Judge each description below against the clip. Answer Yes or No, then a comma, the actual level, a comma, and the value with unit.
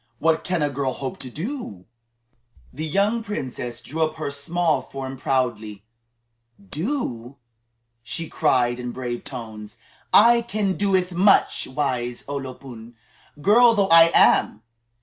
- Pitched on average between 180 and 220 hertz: No, medium, 140 Hz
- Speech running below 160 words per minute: Yes, slow, 135 wpm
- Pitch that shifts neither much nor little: No, wide, 6.8 semitones